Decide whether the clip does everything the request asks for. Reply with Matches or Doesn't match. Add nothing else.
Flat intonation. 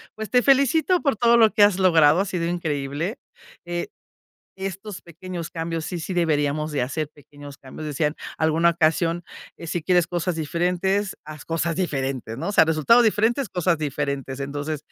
Doesn't match